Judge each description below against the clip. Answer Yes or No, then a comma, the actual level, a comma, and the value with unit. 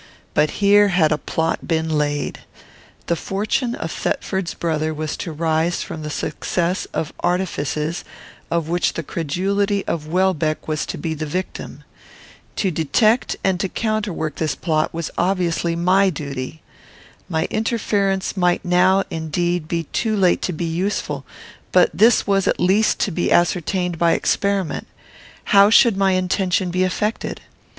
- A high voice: No, medium, 175 Hz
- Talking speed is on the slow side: No, average, 150 wpm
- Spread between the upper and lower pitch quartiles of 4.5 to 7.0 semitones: No, average, 3.5 semitones